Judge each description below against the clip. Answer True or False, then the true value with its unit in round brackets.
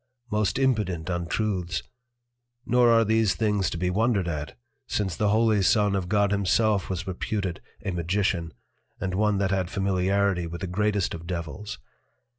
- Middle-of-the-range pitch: False (100 Hz)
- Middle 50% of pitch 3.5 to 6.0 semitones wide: False (2.9 semitones)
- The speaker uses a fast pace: False (155 wpm)